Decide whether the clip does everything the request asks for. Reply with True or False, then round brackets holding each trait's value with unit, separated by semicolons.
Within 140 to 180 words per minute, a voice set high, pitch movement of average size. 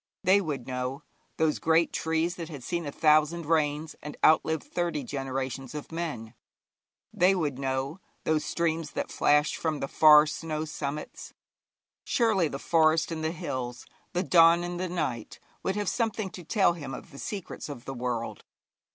False (170 wpm; 155 Hz; 3.4 semitones)